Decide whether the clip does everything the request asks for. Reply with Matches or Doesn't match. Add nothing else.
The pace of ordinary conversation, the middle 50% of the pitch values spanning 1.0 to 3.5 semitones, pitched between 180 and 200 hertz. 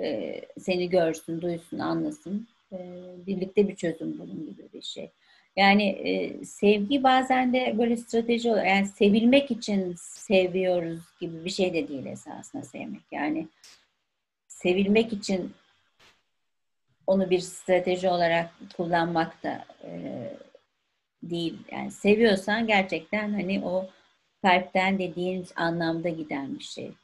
Matches